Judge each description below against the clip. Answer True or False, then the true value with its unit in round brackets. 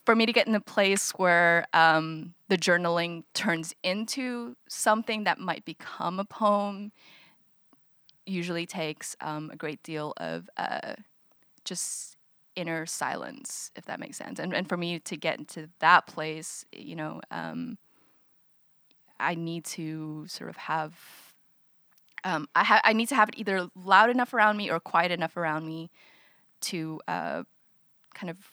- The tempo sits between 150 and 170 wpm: True (155 wpm)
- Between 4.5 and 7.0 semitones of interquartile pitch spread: False (4.1 semitones)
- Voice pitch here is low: False (175 Hz)